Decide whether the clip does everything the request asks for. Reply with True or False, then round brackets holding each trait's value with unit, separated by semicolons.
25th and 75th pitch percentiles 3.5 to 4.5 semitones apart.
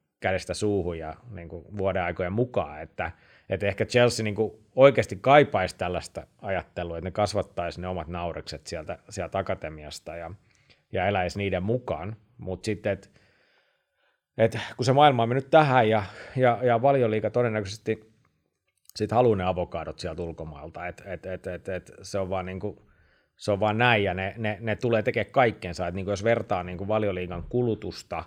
True (3.9 semitones)